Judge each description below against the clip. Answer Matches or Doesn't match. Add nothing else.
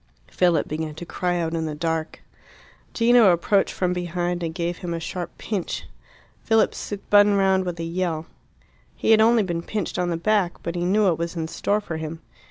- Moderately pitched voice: Matches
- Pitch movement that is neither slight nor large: Matches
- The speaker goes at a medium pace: Matches